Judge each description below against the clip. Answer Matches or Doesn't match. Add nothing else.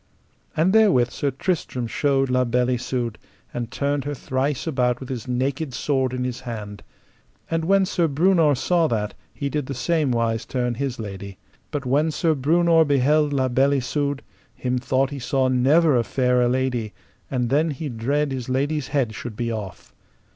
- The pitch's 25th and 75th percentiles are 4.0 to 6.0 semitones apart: Doesn't match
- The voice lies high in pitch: Doesn't match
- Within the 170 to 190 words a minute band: Matches